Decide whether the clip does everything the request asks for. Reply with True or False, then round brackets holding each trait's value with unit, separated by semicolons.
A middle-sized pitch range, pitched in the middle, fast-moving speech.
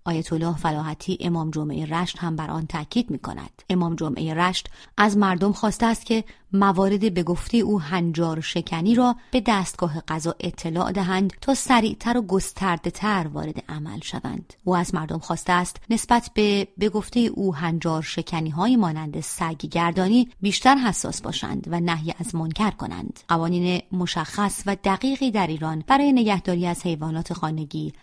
True (3.9 semitones; 180 Hz; 160 wpm)